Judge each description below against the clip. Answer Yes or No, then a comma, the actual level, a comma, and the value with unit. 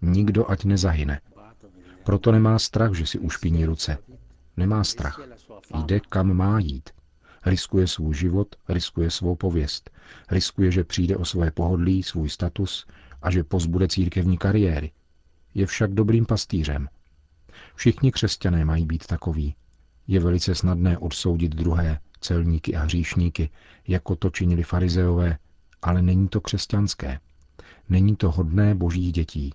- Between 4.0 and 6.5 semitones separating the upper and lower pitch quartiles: No, average, 3.2 semitones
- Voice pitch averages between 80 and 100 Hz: Yes, very low, 90 Hz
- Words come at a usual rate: Yes, average, 130 wpm